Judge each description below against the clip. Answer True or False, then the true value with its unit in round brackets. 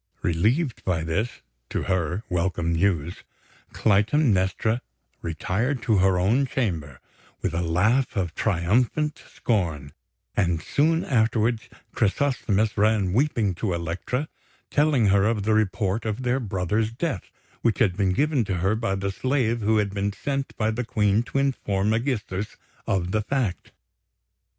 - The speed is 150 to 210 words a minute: False (140 wpm)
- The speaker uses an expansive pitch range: False (4.6 semitones)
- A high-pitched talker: False (105 Hz)